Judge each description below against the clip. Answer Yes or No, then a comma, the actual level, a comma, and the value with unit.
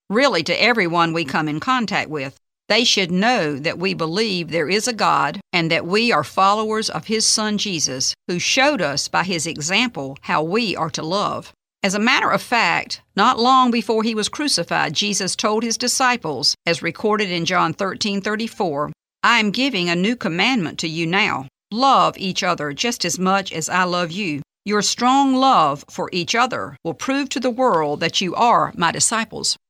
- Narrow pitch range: No, wide, 5.5 semitones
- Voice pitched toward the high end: Yes, high, 195 Hz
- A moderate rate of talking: Yes, average, 190 wpm